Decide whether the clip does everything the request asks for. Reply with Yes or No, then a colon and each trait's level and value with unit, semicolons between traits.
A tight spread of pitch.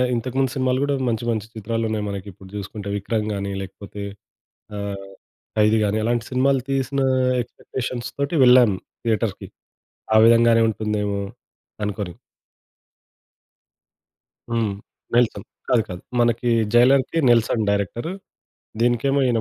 No: average, 3.1 semitones